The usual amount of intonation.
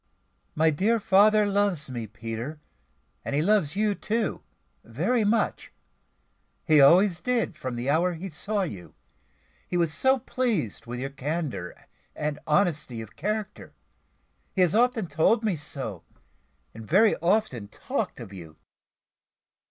No: wide, 7.3 semitones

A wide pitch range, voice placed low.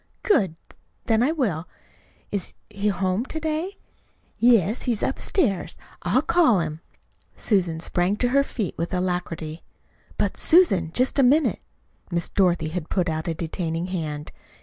No: wide, 6.6 semitones; high, 190 Hz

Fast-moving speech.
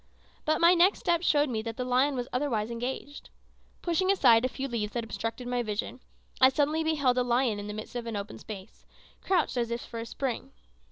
Yes: fast, 215 wpm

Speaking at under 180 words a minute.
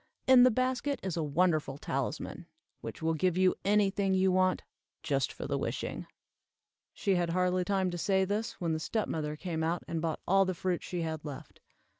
No: average, 200 wpm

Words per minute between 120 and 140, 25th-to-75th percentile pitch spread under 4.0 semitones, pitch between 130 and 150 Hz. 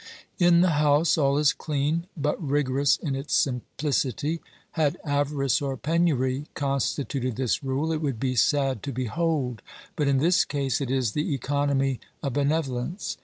No: average, 160 wpm; narrow, 2.4 semitones; medium, 140 Hz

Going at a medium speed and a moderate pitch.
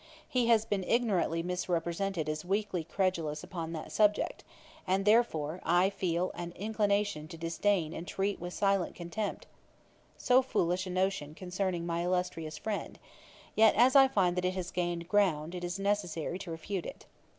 Yes: average, 160 wpm; medium, 180 Hz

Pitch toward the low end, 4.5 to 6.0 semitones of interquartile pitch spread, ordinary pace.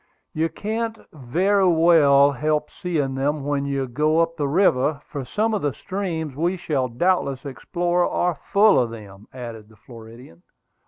No: medium, 150 Hz; average, 5.2 semitones; average, 160 wpm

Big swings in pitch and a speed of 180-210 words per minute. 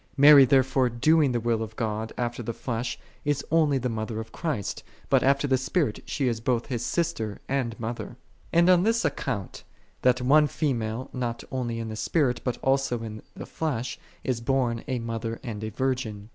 No: average, 3.2 semitones; average, 190 wpm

